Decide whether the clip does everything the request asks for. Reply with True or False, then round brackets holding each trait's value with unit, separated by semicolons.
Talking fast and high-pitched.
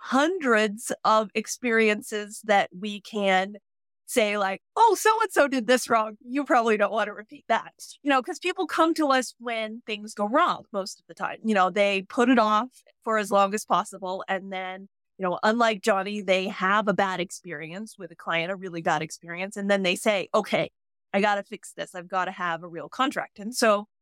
True (210 wpm; 210 Hz)